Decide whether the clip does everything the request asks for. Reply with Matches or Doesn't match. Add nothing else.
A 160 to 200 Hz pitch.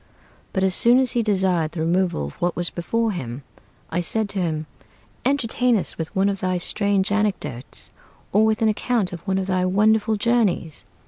Matches